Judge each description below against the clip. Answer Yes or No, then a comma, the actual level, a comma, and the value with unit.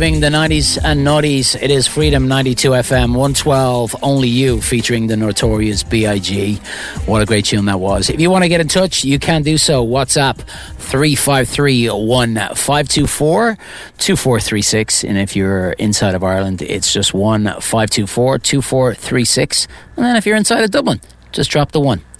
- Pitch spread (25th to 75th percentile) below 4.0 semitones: No, average, 5.3 semitones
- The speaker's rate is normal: Yes, average, 155 wpm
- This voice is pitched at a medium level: No, low, 125 Hz